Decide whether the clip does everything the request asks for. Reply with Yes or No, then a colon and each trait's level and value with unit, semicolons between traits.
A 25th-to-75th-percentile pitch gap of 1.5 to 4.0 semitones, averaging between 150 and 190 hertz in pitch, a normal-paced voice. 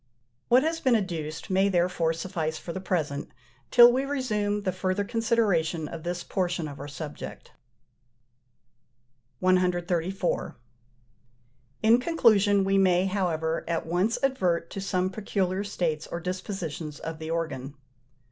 No: average, 3.7 semitones; medium, 185 Hz; slow, 130 wpm